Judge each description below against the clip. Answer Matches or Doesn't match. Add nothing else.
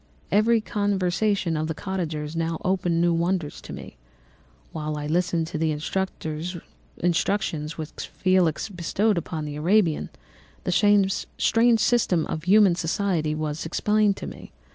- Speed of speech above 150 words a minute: Doesn't match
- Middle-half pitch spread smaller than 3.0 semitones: Doesn't match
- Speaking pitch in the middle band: Matches